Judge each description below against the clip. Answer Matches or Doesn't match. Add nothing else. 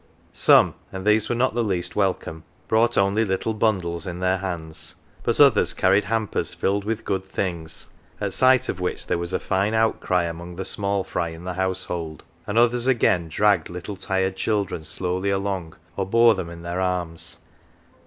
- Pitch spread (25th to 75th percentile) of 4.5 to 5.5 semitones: Doesn't match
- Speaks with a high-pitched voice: Doesn't match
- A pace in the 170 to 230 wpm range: Matches